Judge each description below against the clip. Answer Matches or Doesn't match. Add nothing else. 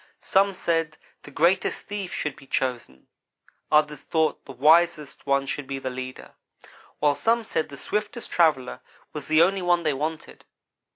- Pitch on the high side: Doesn't match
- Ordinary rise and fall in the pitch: Matches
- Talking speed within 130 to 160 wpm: Matches